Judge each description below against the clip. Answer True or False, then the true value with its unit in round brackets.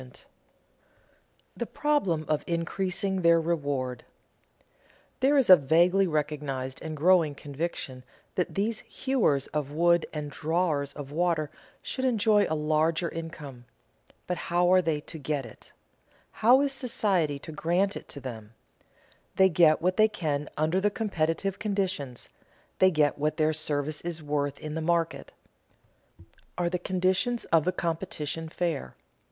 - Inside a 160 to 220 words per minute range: False (145 wpm)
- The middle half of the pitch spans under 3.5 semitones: False (3.8 semitones)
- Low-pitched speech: False (165 Hz)